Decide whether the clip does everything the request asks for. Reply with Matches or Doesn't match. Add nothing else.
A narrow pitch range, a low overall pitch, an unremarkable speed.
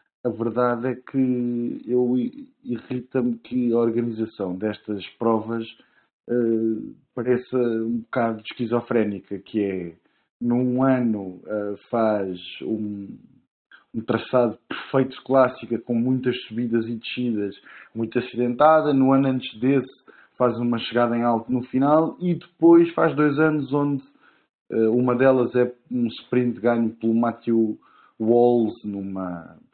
Matches